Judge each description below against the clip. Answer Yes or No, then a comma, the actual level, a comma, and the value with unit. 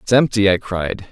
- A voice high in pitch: No, low, 105 Hz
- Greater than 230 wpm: No, fast, 215 wpm